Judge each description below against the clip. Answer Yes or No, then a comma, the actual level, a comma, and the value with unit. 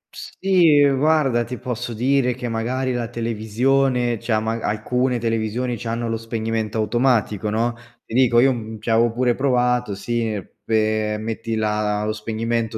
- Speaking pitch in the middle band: No, low, 115 Hz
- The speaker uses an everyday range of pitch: No, narrow, 2.2 semitones